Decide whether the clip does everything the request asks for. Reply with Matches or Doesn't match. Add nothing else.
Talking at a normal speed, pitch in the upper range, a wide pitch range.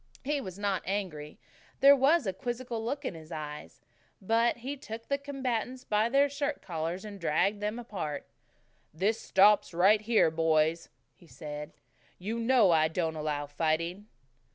Matches